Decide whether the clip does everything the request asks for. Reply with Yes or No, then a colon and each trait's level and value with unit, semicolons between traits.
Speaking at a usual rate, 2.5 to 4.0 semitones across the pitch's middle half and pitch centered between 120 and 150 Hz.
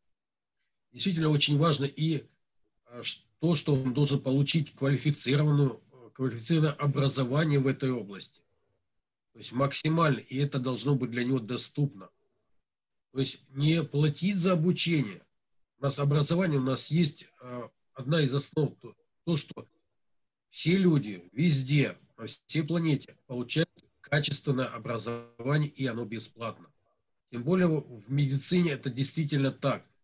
Yes: average, 125 wpm; average, 3.2 semitones; medium, 140 Hz